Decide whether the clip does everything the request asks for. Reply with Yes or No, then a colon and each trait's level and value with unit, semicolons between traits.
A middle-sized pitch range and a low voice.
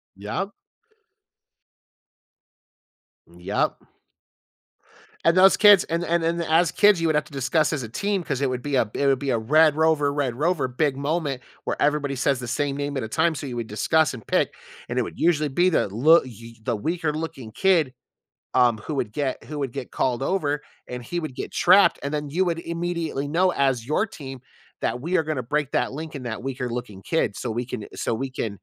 No: average, 4.5 semitones; medium, 145 Hz